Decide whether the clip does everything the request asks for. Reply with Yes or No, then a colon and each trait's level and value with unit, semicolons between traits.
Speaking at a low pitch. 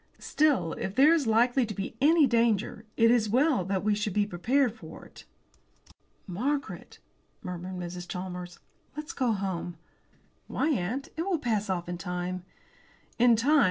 No: high, 215 Hz